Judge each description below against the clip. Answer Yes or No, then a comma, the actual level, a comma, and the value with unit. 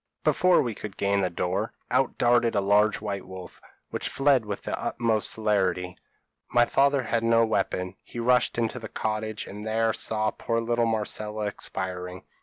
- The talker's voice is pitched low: Yes, low, 110 Hz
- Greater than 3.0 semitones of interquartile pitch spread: No, average, 2.7 semitones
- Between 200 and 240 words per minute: No, average, 170 wpm